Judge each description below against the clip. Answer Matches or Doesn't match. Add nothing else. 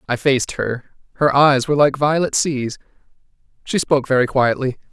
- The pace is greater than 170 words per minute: Doesn't match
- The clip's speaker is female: Doesn't match